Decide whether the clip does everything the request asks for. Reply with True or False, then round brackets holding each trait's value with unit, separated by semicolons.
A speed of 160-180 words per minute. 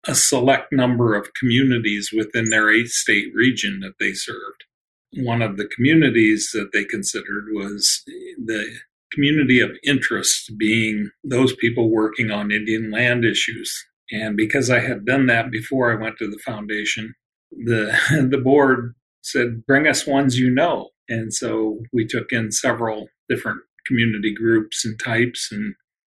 False (150 wpm)